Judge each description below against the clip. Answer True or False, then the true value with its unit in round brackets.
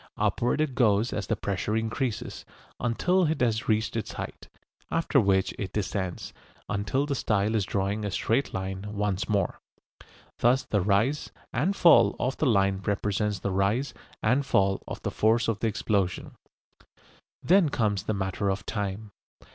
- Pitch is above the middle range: False (105 Hz)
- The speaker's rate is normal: True (160 wpm)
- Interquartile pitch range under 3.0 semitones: False (3.8 semitones)